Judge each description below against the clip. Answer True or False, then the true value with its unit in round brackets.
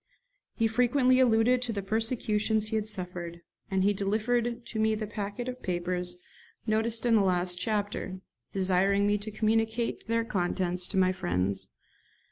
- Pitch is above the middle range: True (210 Hz)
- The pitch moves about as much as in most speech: True (3.4 semitones)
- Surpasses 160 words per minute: False (155 wpm)